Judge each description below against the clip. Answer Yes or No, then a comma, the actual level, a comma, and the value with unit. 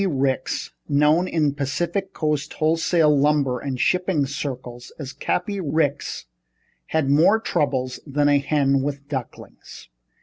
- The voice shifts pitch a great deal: No, narrow, 2.5 semitones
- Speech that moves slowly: Yes, slow, 125 wpm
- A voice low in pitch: No, medium, 145 Hz